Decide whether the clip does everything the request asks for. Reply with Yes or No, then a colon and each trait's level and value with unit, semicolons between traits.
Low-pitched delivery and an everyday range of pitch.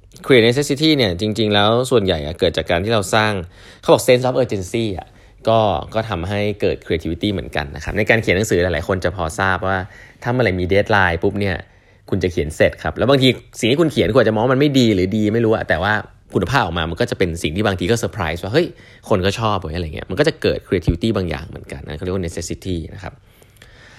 Yes: low, 100 Hz; average, 3.9 semitones